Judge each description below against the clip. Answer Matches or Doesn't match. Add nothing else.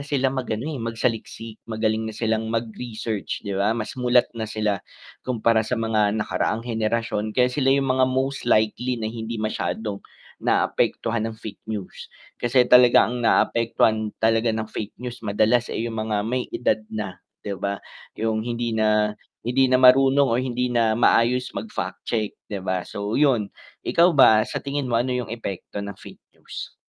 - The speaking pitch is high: Doesn't match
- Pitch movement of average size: Doesn't match